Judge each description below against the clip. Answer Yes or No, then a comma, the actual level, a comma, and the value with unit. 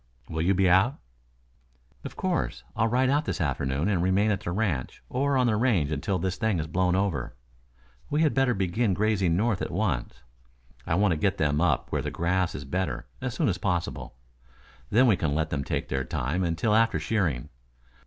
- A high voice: No, very low, 95 Hz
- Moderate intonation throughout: No, wide, 5.7 semitones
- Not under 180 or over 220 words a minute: Yes, average, 200 wpm